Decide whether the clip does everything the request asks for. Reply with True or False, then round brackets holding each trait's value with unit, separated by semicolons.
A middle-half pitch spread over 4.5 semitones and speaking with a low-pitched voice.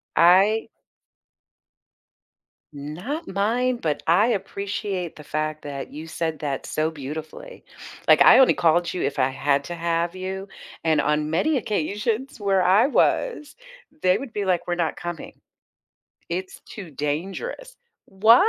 False (5.3 semitones; 180 Hz)